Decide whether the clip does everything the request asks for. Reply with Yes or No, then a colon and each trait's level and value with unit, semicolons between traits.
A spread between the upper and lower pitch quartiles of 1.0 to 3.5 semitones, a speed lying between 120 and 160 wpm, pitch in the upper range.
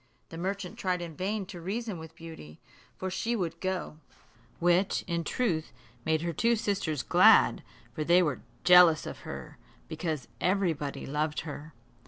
No: average, 3.1 semitones; average, 155 wpm; medium, 170 Hz